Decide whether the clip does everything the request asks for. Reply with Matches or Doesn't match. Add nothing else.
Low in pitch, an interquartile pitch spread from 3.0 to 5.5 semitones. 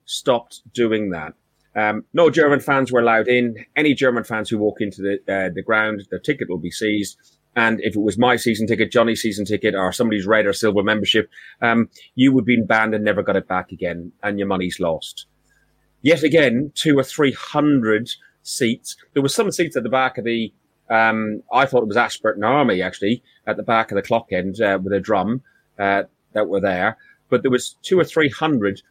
Matches